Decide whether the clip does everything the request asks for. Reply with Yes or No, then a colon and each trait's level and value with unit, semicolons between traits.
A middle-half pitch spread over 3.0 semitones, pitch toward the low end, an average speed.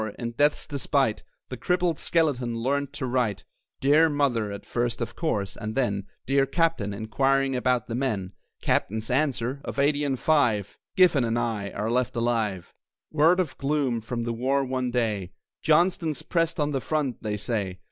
Yes: average, 4.1 semitones; low, 125 Hz; average, 165 wpm